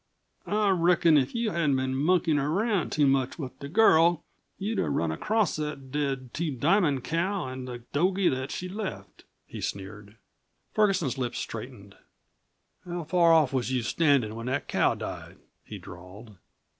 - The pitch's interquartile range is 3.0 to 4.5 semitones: No, wide, 5.5 semitones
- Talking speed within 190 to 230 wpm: No, average, 160 wpm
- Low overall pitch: No, medium, 145 Hz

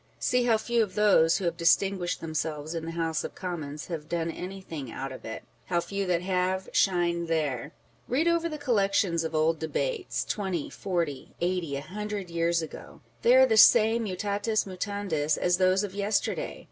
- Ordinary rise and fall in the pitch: Yes, average, 3.9 semitones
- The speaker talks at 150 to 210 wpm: Yes, average, 180 wpm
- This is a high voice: No, medium, 180 Hz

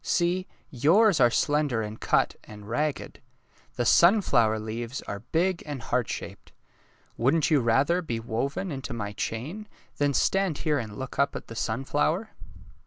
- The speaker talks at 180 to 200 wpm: No, average, 155 wpm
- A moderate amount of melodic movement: No, wide, 6.1 semitones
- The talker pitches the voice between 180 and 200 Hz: No, low, 135 Hz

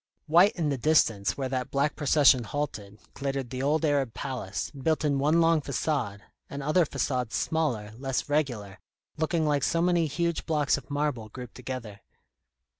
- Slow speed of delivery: No, average, 165 wpm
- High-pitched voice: No, medium, 140 Hz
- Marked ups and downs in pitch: No, average, 3.6 semitones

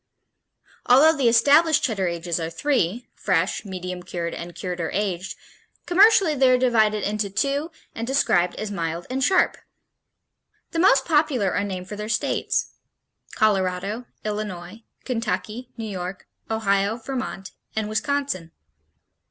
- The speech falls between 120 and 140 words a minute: Yes, slow, 135 wpm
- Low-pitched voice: No, high, 215 Hz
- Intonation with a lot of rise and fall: Yes, wide, 5.9 semitones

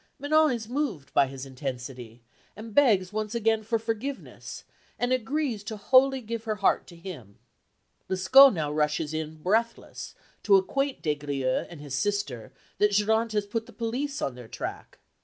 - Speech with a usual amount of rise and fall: No, wide, 7.6 semitones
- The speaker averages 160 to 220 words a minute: Yes, average, 165 wpm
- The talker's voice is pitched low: No, high, 210 Hz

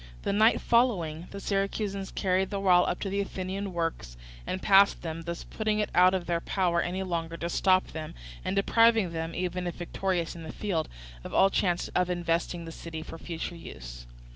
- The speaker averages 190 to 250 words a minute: Yes, average, 195 wpm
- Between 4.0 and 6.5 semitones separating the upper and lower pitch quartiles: No, average, 2.7 semitones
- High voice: No, medium, 180 Hz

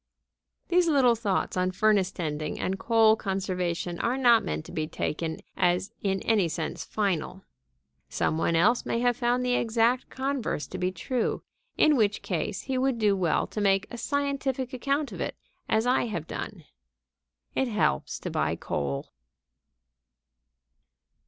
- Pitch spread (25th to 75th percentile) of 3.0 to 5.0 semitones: No, wide, 5.4 semitones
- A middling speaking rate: Yes, average, 155 wpm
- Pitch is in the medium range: No, high, 210 Hz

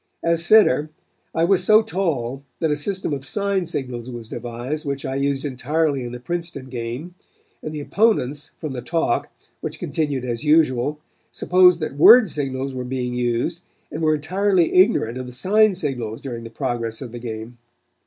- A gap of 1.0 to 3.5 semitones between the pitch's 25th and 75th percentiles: No, average, 5.3 semitones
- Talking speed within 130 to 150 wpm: No, average, 175 wpm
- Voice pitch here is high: No, medium, 140 Hz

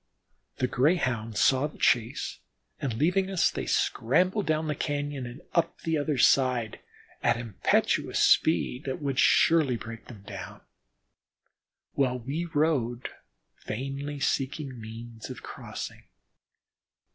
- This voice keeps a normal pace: No, slow, 120 wpm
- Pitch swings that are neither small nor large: Yes, average, 4.2 semitones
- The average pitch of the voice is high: No, low, 135 Hz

